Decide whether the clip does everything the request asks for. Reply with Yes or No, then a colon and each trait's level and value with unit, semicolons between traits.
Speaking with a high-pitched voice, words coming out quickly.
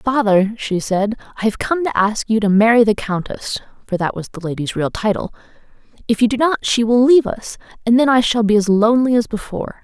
Yes: high, 220 Hz; fast, 215 wpm